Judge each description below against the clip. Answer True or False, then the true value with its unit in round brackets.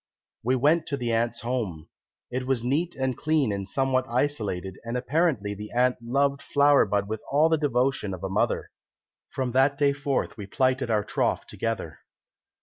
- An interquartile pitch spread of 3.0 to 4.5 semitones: True (4.2 semitones)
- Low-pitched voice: True (130 Hz)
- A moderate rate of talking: True (175 wpm)